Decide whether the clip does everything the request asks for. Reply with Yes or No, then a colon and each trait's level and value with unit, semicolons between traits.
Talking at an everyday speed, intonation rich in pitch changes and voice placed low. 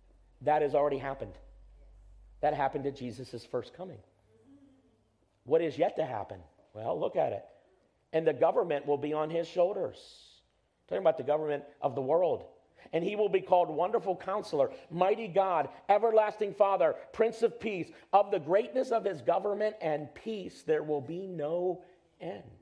No: average, 165 wpm; wide, 6.1 semitones; medium, 180 Hz